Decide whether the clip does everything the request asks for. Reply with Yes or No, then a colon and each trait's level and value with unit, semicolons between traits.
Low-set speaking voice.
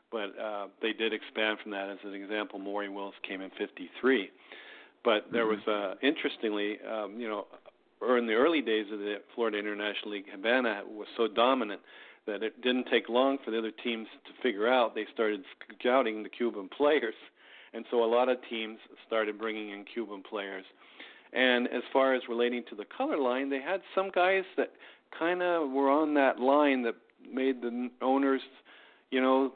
Yes: low, 115 Hz